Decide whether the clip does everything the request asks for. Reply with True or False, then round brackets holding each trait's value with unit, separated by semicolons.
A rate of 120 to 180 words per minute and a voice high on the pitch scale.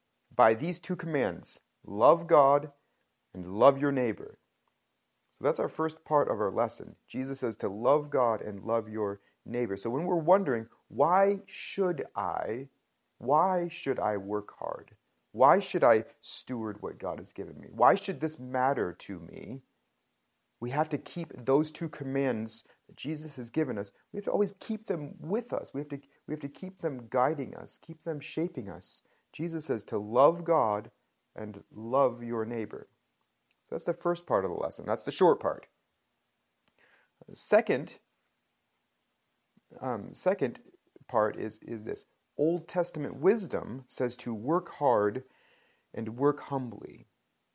False (160 wpm; 140 Hz)